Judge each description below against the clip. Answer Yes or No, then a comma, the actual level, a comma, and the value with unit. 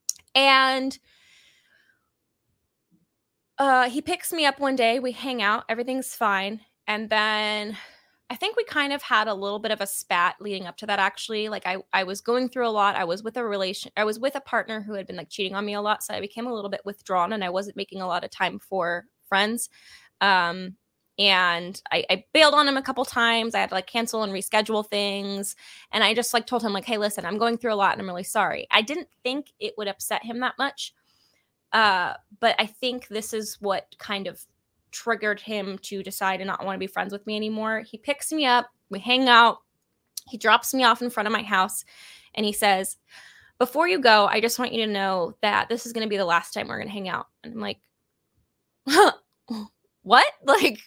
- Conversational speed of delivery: No, fast, 220 wpm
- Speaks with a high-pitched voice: Yes, high, 215 Hz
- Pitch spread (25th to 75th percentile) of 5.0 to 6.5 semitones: No, average, 3.7 semitones